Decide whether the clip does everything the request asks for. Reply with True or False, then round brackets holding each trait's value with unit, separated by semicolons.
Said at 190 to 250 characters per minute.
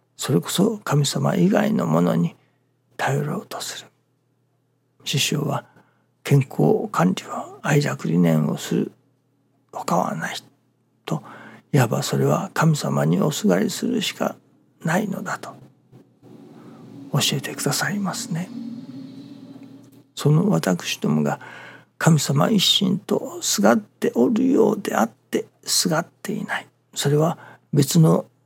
True (225 characters per minute)